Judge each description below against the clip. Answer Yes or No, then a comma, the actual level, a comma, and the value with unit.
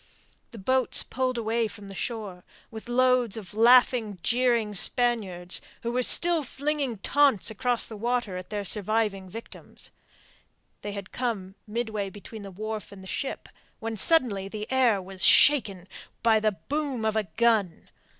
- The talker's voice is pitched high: Yes, high, 220 Hz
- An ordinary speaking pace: Yes, average, 160 wpm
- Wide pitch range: No, average, 3.6 semitones